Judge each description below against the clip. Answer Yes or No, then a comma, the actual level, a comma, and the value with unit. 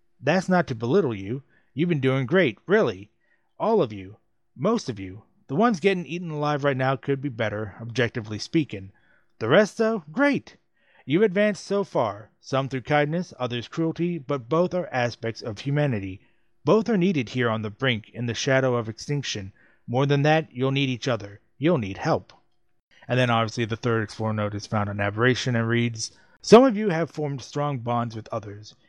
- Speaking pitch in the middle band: No, low, 130 Hz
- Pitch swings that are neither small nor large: No, wide, 6.1 semitones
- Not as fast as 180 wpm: No, average, 190 wpm